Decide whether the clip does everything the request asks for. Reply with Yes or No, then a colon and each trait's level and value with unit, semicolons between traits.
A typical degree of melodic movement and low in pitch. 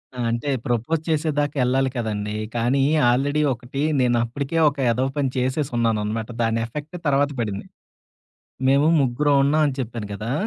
Yes: average, 3.6 semitones; low, 130 Hz